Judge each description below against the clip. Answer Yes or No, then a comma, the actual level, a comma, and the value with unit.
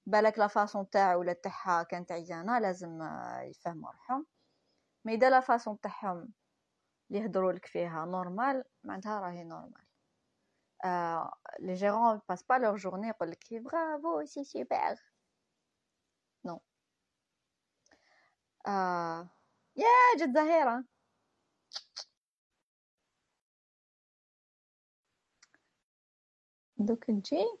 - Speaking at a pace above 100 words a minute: No, average, 90 wpm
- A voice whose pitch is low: No, high, 210 Hz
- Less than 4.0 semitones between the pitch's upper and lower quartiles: No, wide, 5.5 semitones